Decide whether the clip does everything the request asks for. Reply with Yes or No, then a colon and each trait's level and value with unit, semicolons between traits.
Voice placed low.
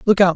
No: high, 195 Hz